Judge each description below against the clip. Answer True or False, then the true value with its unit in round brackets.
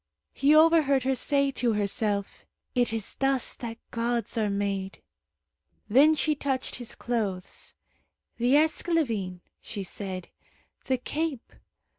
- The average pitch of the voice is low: False (240 Hz)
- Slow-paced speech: True (120 wpm)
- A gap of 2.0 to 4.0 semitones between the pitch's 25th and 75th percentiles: False (5.3 semitones)